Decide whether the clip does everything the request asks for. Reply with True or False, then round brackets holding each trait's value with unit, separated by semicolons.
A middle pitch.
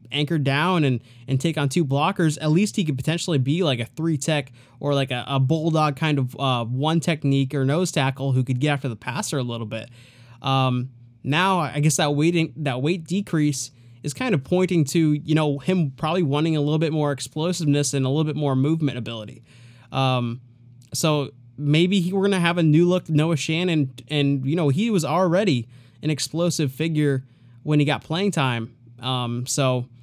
True (145 Hz)